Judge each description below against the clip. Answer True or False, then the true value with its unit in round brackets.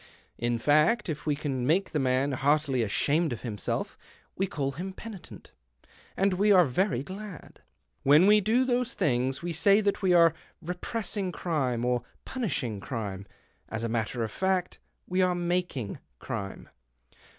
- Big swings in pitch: True (7.0 semitones)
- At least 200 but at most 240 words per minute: False (160 wpm)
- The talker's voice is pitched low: False (155 Hz)